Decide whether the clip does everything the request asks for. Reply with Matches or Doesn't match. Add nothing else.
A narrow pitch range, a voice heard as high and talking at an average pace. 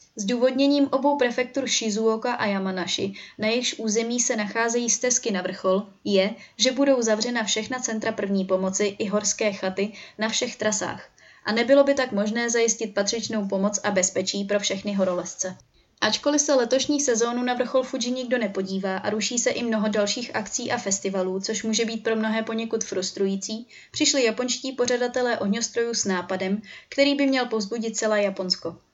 Doesn't match